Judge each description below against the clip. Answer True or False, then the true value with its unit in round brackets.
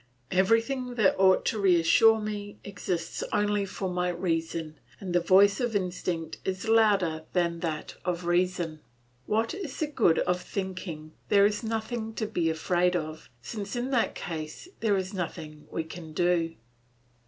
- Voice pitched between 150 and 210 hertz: True (185 Hz)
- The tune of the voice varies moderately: True (4.0 semitones)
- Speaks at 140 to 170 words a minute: True (155 wpm)